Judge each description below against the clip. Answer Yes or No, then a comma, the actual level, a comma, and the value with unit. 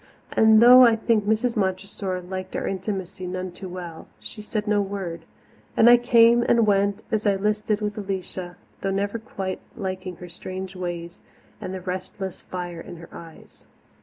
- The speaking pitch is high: Yes, high, 195 Hz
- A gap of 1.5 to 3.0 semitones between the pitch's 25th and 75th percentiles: Yes, narrow, 2.5 semitones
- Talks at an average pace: Yes, average, 170 wpm